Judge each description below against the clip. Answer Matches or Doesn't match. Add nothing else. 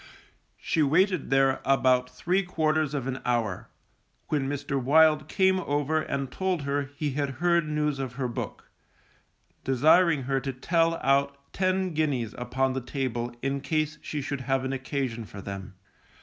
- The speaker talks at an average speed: Matches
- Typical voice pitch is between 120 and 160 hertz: Matches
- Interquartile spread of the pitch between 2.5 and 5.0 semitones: Matches